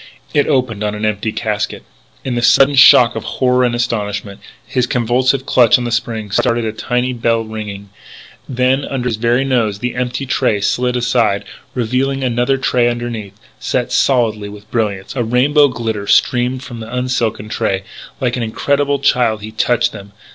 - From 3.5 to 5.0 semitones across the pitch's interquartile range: No, average, 2.7 semitones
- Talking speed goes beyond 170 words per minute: Yes, average, 185 wpm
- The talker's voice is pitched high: No, low, 120 Hz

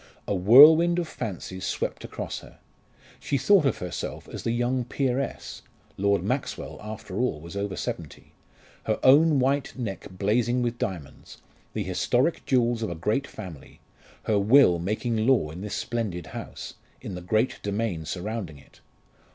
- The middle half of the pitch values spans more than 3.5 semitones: Yes, wide, 5.4 semitones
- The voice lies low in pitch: Yes, low, 110 Hz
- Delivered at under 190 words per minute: Yes, average, 155 wpm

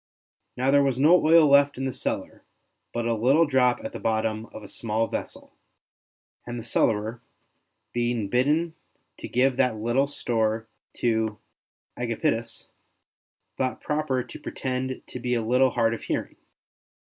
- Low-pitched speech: Yes, low, 125 Hz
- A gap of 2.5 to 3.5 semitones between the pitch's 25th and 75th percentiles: Yes, average, 2.9 semitones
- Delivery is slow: No, average, 150 wpm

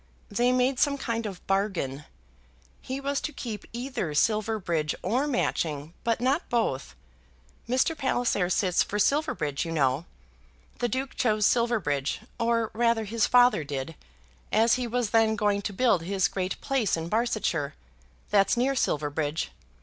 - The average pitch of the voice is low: No, high, 220 Hz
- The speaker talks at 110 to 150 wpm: Yes, average, 145 wpm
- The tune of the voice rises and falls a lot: Yes, wide, 6.3 semitones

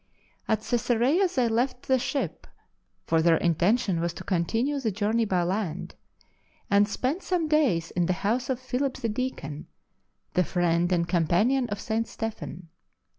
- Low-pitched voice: No, high, 220 Hz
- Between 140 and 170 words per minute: Yes, average, 160 wpm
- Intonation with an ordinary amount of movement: No, wide, 6.4 semitones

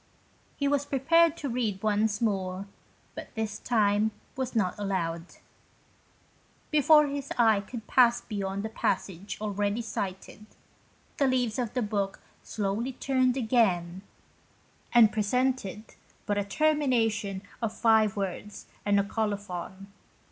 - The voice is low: No, high, 215 Hz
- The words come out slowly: Yes, slow, 130 wpm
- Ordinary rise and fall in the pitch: Yes, average, 4.0 semitones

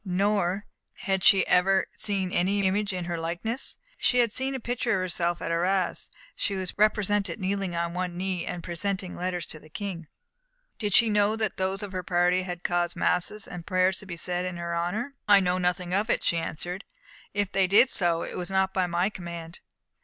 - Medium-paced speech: No, fast, 210 wpm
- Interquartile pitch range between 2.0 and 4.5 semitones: Yes, narrow, 2.4 semitones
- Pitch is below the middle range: No, medium, 185 Hz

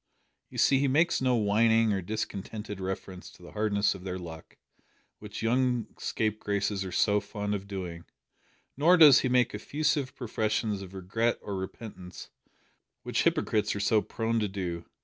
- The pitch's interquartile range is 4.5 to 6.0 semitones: No, average, 3.2 semitones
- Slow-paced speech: No, average, 160 wpm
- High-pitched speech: No, low, 105 Hz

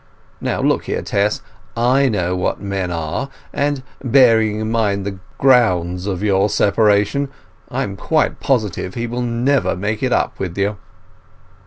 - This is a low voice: Yes, low, 105 Hz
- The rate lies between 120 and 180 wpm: Yes, average, 155 wpm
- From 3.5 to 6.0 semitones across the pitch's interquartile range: Yes, average, 4.1 semitones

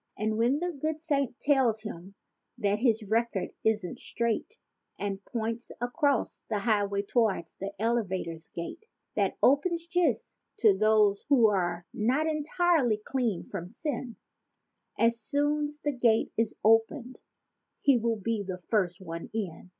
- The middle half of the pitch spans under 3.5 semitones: No, average, 5.2 semitones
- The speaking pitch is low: No, high, 225 Hz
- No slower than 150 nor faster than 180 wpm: No, average, 140 wpm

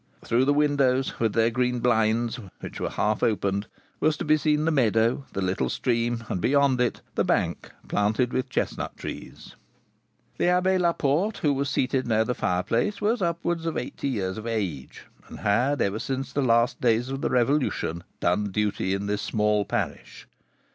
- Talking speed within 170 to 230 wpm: Yes, average, 175 wpm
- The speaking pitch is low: Yes, low, 120 Hz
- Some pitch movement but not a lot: Yes, average, 5.0 semitones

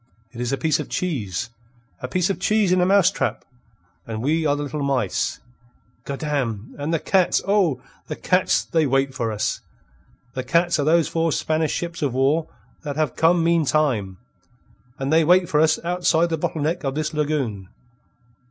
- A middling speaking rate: Yes, average, 180 wpm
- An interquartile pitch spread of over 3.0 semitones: Yes, average, 3.8 semitones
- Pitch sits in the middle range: Yes, medium, 155 Hz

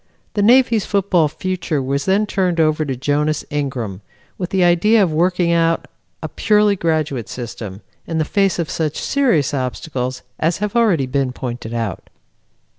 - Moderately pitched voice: Yes, medium, 160 Hz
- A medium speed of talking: Yes, average, 160 wpm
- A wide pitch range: Yes, wide, 5.8 semitones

